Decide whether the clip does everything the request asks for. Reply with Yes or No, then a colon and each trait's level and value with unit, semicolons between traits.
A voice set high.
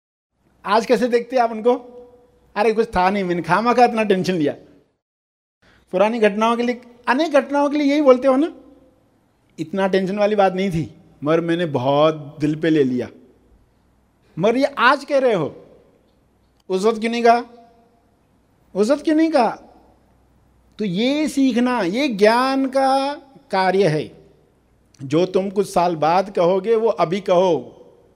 Yes: high, 220 Hz